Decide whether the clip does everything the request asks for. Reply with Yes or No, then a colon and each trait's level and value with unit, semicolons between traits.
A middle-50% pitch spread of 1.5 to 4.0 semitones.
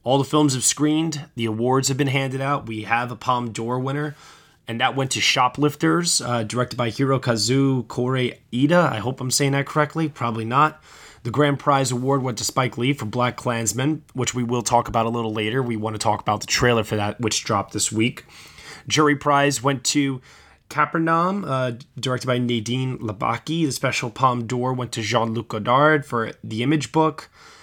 Yes: average, 3.5 semitones